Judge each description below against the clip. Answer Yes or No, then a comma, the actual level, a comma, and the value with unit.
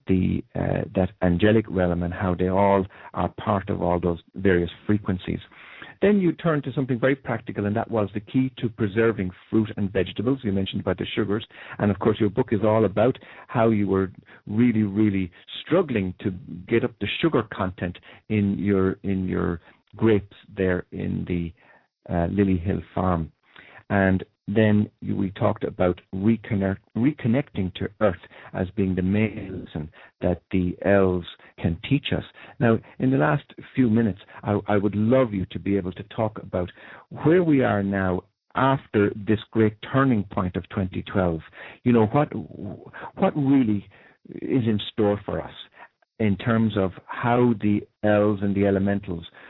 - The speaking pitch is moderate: No, low, 105 Hz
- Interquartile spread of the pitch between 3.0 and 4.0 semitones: Yes, average, 3.4 semitones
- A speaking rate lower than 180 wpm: Yes, average, 165 wpm